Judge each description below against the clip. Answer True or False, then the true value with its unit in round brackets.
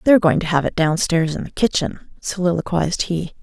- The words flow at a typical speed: True (195 wpm)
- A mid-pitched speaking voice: True (170 Hz)